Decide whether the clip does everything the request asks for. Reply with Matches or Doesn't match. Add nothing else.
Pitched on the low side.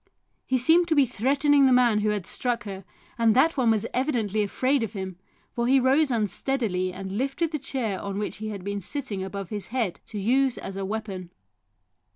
Doesn't match